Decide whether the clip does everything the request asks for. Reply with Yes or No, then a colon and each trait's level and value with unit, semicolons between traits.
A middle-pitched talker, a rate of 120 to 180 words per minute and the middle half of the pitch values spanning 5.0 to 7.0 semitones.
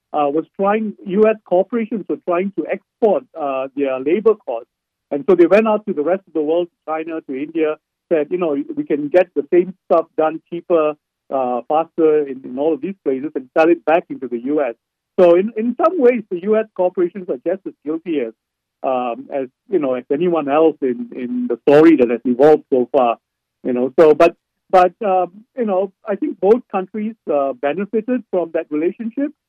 No: medium, 165 Hz; average, 195 wpm; wide, 5.4 semitones